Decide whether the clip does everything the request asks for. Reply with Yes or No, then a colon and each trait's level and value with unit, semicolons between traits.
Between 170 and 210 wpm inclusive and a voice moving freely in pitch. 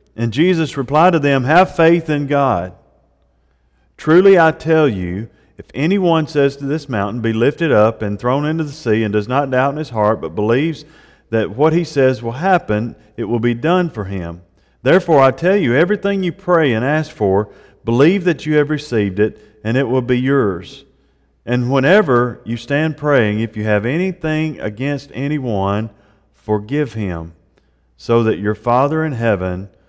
Yes: average, 175 wpm; wide, 6.5 semitones